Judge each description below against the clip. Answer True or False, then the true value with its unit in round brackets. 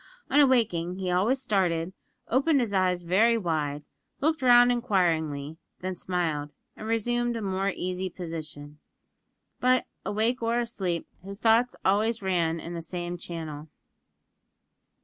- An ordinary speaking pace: False (130 wpm)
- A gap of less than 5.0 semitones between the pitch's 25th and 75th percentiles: False (5.6 semitones)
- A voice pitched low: False (190 Hz)